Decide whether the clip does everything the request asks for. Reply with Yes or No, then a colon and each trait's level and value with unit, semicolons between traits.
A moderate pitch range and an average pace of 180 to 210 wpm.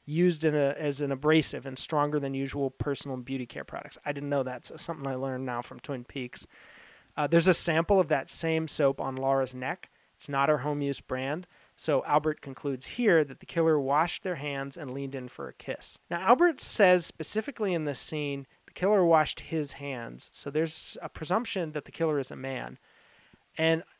Yes: average, 3.1 semitones; fast, 205 wpm